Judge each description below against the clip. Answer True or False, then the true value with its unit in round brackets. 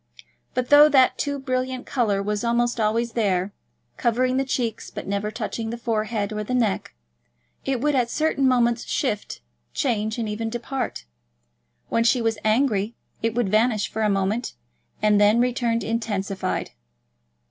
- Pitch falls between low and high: False (230 Hz)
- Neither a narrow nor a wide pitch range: True (3.0 semitones)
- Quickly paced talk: False (155 wpm)